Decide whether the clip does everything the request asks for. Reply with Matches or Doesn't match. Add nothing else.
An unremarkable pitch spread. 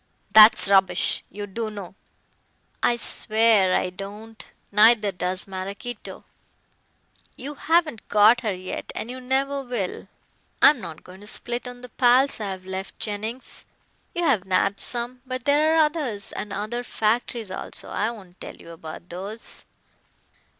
Matches